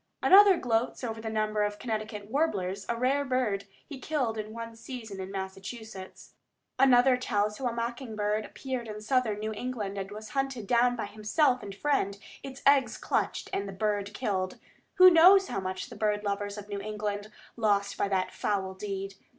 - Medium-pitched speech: No, high, 215 Hz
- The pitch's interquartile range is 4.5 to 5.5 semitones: No, average, 3.7 semitones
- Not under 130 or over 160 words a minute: No, average, 185 wpm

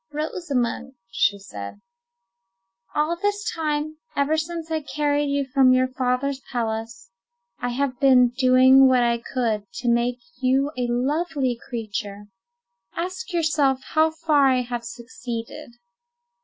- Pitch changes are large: No, average, 3.8 semitones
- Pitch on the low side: No, very high, 260 Hz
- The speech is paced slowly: Yes, slow, 130 wpm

